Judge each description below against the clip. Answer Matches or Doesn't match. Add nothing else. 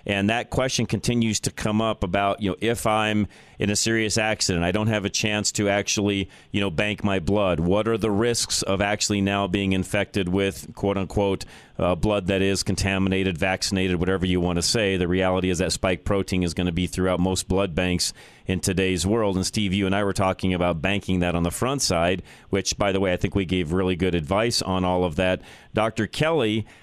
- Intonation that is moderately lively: Doesn't match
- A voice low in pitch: Matches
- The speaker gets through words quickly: Matches